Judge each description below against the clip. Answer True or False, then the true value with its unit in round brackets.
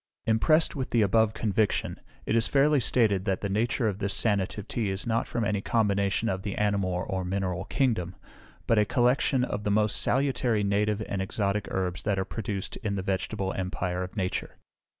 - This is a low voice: True (105 Hz)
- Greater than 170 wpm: True (190 wpm)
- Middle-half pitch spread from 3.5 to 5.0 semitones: False (2.9 semitones)